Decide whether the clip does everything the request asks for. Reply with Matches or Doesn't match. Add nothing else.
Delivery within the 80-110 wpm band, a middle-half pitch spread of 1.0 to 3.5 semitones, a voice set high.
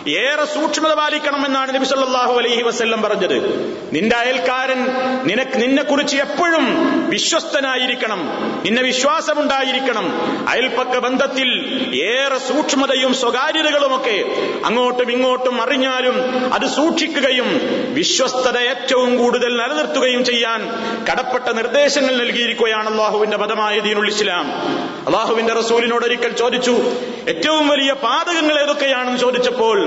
Matches